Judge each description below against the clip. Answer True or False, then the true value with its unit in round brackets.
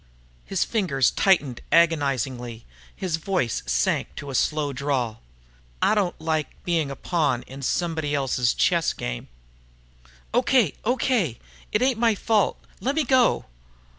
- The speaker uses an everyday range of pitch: False (6.8 semitones)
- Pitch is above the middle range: False (160 Hz)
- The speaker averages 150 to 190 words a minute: False (135 wpm)